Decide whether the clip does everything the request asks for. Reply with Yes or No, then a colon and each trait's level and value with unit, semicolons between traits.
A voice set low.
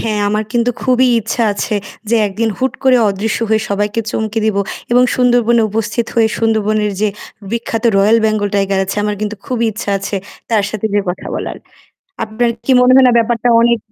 No: high, 220 Hz